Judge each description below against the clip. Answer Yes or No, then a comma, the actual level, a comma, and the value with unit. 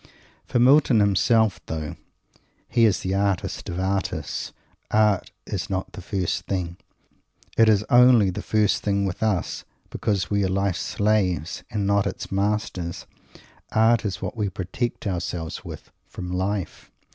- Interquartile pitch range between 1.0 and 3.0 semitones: Yes, average, 2.7 semitones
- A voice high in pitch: No, low, 100 Hz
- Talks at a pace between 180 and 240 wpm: No, average, 145 wpm